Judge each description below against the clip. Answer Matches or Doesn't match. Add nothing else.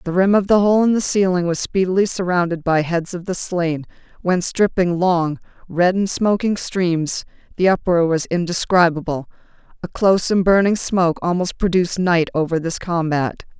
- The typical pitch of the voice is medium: Matches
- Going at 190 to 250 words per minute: Doesn't match